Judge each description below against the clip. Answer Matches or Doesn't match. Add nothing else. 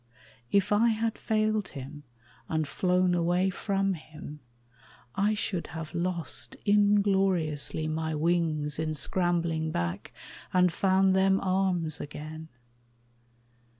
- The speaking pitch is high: Doesn't match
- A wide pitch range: Doesn't match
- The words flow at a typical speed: Doesn't match